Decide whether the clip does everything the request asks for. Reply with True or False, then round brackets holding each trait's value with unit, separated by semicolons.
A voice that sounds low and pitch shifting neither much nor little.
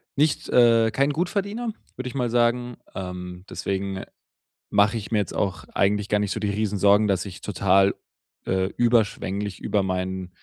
True (105 Hz; 3.9 semitones)